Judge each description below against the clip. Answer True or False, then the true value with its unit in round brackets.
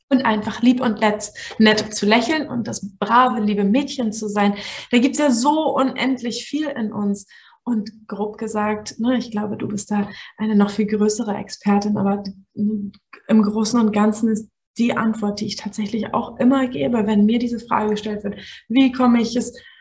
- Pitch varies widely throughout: False (2.6 semitones)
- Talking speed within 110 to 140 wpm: False (185 wpm)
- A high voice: True (220 Hz)